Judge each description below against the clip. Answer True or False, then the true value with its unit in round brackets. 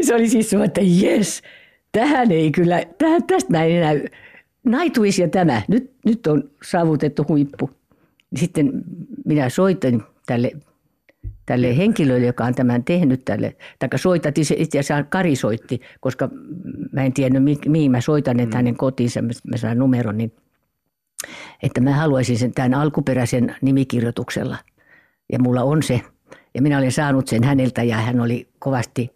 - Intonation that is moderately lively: False (5.8 semitones)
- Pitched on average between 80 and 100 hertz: False (140 Hz)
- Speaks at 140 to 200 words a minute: True (150 wpm)